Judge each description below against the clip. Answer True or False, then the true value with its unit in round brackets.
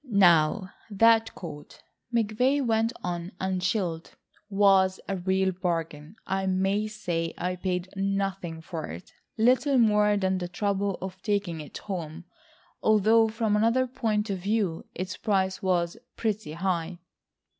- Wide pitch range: False (3.2 semitones)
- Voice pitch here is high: True (195 Hz)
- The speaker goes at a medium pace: False (130 wpm)